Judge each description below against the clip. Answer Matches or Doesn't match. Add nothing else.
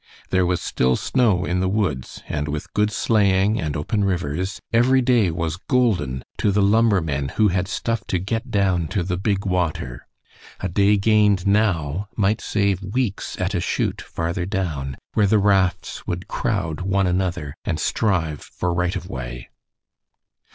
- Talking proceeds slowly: Doesn't match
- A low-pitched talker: Matches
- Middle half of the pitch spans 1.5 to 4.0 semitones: Matches